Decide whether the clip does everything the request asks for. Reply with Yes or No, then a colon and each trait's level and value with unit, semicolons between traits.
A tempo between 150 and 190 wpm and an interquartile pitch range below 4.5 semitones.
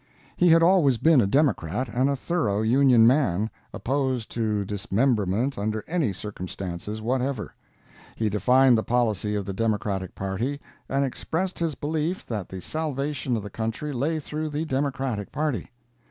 No: average, 155 wpm; wide, 5.4 semitones